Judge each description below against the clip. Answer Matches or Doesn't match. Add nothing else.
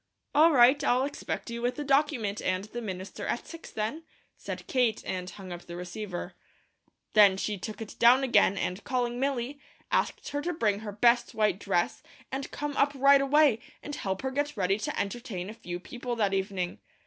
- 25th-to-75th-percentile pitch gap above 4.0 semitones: Matches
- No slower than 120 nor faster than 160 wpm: Doesn't match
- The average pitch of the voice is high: Matches